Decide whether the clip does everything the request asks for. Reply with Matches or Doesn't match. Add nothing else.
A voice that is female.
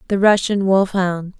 Matches